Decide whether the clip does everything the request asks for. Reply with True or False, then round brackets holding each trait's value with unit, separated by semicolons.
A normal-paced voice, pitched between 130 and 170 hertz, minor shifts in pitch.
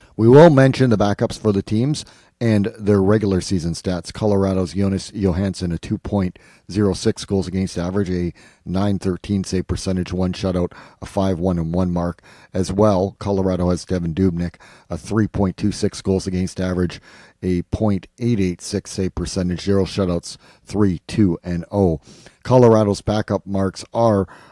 False (170 wpm; 95 Hz; 2.2 semitones)